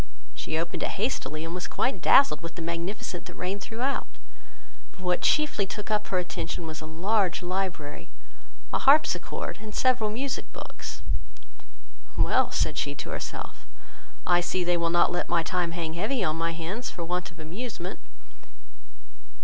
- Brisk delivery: No, average, 165 wpm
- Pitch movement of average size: Yes, average, 4.0 semitones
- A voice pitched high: No, medium, 180 Hz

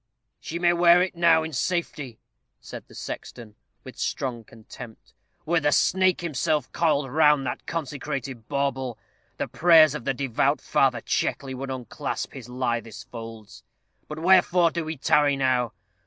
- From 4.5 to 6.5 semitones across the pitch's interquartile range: Yes, average, 4.8 semitones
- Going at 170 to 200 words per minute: No, average, 150 wpm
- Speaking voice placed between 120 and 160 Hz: Yes, medium, 140 Hz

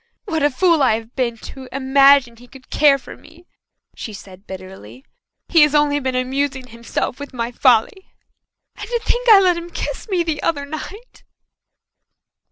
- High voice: Yes, very high, 275 Hz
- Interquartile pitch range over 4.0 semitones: Yes, average, 5.0 semitones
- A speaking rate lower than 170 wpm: No, average, 175 wpm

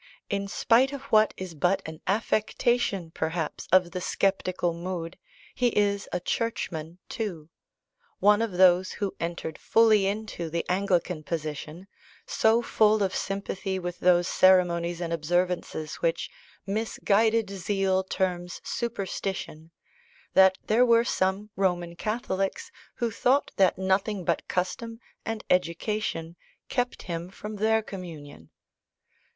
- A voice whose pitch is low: No, high, 190 Hz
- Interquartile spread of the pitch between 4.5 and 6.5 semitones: No, average, 3.6 semitones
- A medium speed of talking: No, slow, 125 wpm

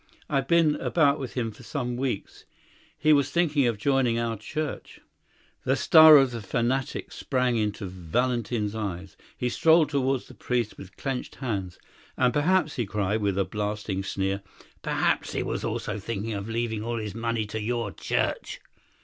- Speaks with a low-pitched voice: Yes, low, 115 Hz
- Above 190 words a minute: No, average, 165 wpm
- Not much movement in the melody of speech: No, average, 4.4 semitones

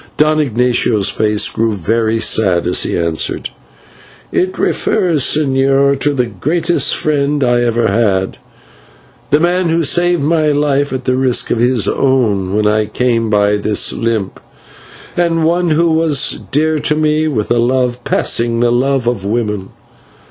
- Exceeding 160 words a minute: No, average, 155 wpm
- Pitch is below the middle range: Yes, low, 125 Hz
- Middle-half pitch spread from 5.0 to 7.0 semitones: Yes, wide, 5.4 semitones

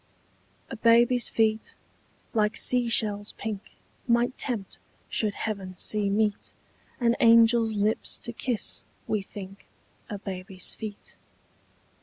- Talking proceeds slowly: Yes, slow, 115 wpm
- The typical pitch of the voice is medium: No, high, 220 Hz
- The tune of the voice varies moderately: No, narrow, 2.3 semitones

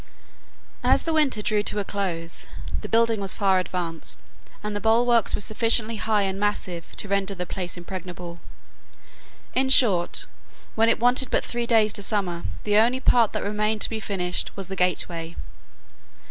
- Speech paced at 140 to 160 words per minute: No, average, 170 wpm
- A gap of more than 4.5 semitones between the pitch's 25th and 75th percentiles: No, average, 3.6 semitones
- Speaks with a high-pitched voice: Yes, high, 205 Hz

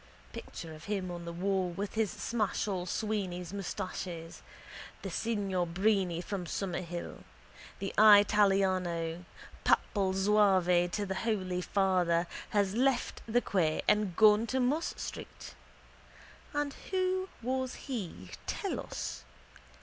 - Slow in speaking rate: Yes, slow, 120 wpm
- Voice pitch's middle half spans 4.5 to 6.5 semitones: No, average, 3.2 semitones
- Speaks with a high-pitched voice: Yes, high, 195 Hz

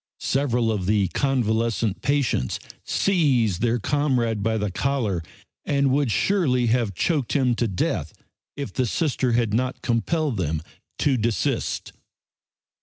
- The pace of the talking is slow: Yes, slow, 130 wpm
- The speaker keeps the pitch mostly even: No, average, 4.1 semitones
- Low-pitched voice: Yes, low, 120 Hz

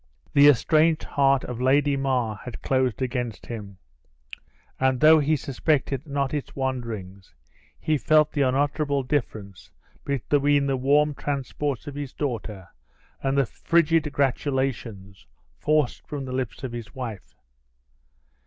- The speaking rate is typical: No, slow, 130 wpm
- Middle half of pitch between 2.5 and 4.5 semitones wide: Yes, average, 2.9 semitones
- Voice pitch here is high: No, low, 135 Hz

